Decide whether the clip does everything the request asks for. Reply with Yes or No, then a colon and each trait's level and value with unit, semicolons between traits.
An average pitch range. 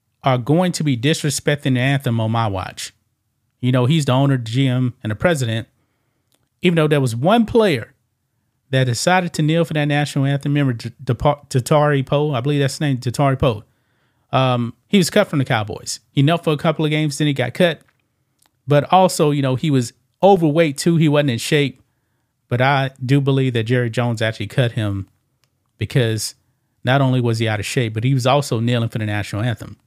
Yes: average, 3.3 semitones